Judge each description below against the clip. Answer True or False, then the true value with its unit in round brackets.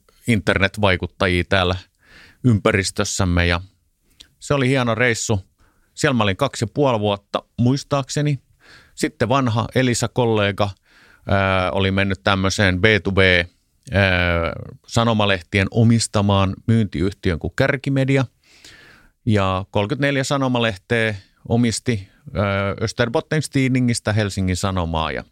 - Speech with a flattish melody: False (4.1 semitones)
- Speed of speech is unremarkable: False (85 wpm)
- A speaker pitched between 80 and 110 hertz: True (105 Hz)